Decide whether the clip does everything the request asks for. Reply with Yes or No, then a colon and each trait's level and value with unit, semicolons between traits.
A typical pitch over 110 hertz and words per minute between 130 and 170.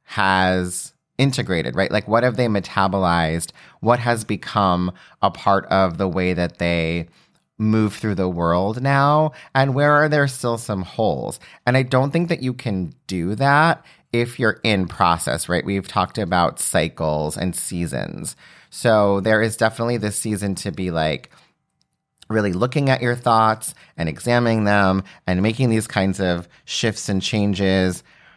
No: low, 105 Hz; average, 160 wpm